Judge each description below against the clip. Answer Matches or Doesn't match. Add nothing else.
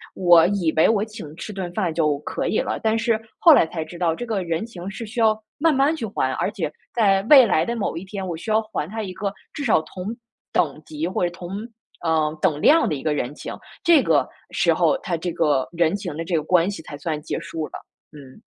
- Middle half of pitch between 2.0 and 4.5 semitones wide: Doesn't match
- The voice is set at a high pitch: Doesn't match